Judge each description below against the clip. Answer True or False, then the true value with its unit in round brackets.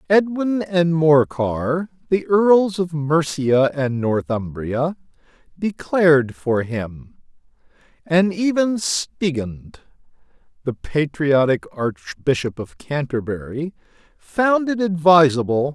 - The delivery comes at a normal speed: False (90 wpm)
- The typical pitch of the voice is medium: True (155 Hz)